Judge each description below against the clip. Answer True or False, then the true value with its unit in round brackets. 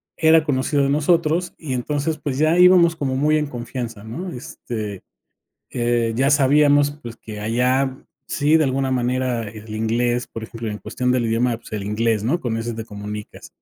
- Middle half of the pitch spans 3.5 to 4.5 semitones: True (4.2 semitones)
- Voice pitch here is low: True (125 Hz)